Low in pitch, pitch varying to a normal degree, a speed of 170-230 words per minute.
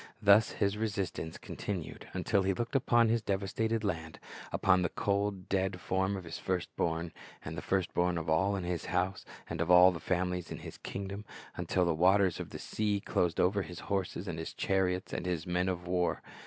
No: very low, 95 Hz; narrow, 2.2 semitones; fast, 205 wpm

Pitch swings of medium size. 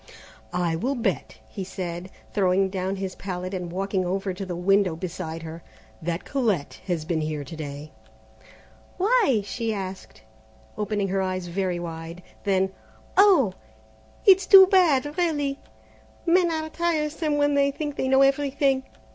No: wide, 8.1 semitones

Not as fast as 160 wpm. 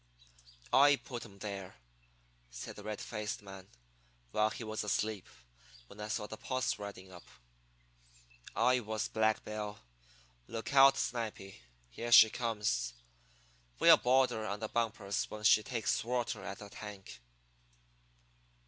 Yes: average, 140 wpm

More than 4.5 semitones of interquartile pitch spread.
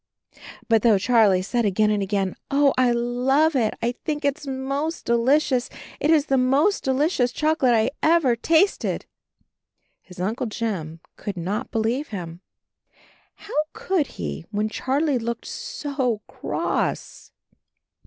Yes: average, 5.0 semitones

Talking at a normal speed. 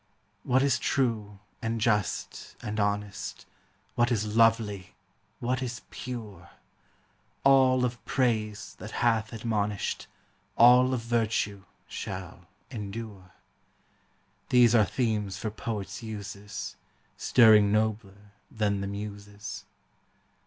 No: slow, 110 wpm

